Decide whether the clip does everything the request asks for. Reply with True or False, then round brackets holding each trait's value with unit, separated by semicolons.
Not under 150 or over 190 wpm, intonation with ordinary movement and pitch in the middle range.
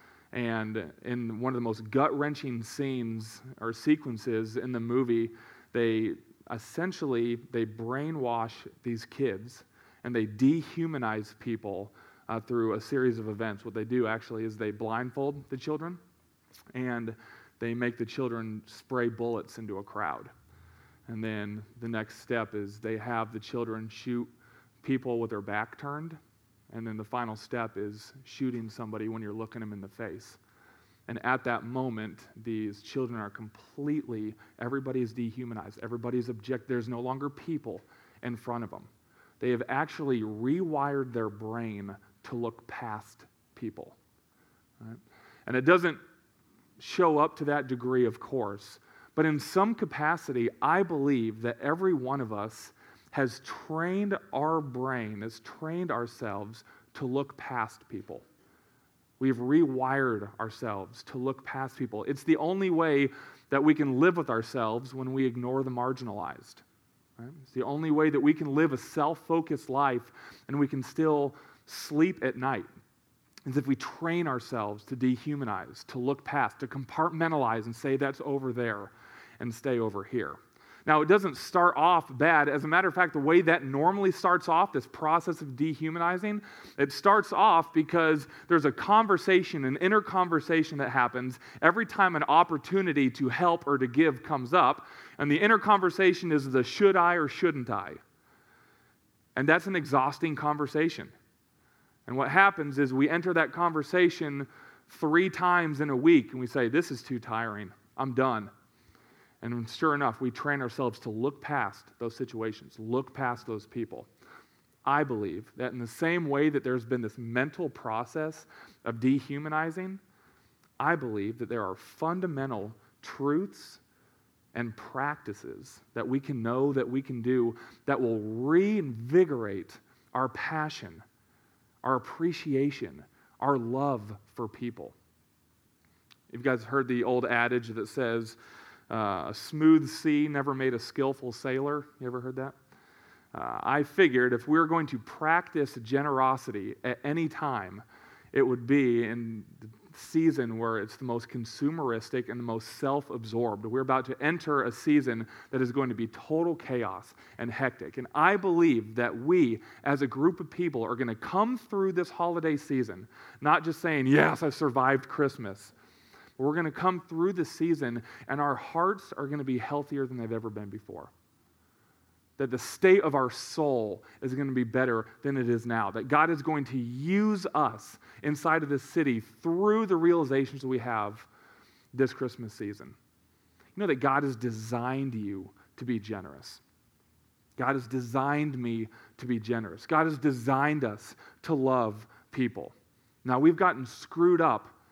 False (160 wpm; 4.6 semitones; 130 Hz)